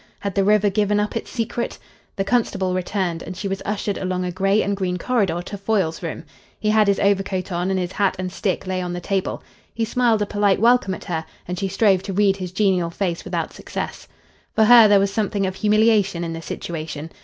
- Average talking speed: No, fast, 225 wpm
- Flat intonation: Yes, narrow, 2.3 semitones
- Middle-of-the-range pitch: No, high, 195 Hz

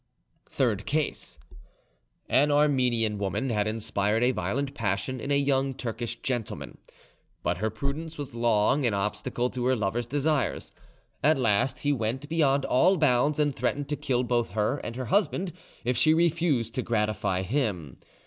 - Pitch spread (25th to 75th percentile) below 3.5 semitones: No, average, 4.6 semitones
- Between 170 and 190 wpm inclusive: No, average, 160 wpm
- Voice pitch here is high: No, low, 125 Hz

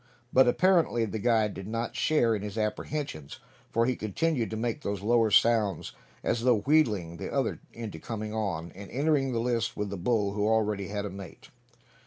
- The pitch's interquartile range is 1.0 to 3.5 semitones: Yes, average, 2.9 semitones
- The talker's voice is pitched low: Yes, low, 110 Hz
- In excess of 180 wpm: Yes, average, 190 wpm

